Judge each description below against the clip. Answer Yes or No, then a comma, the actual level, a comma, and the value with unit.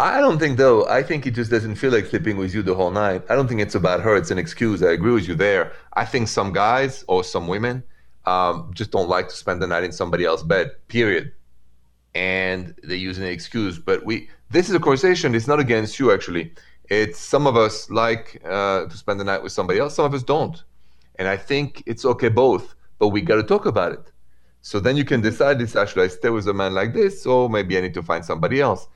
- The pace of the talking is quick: Yes, fast, 245 wpm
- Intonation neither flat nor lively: No, wide, 5.8 semitones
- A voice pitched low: Yes, low, 105 Hz